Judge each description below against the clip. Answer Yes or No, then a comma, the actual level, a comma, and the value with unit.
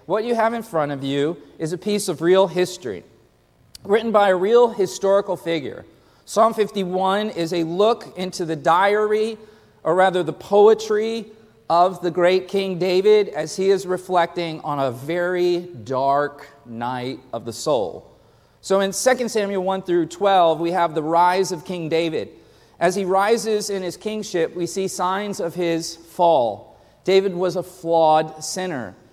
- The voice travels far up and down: No, average, 3.2 semitones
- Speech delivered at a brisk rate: No, average, 165 wpm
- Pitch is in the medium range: Yes, medium, 180 Hz